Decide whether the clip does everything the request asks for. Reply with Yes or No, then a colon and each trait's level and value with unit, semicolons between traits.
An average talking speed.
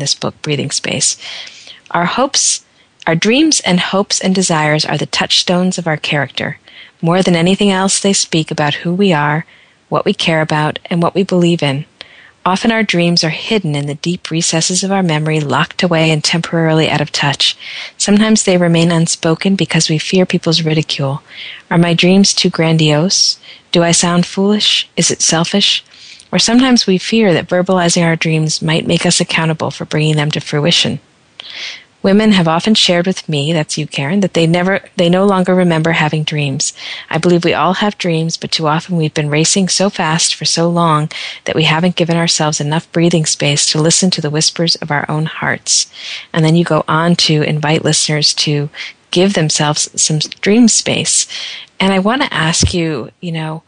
Yes: average, 190 wpm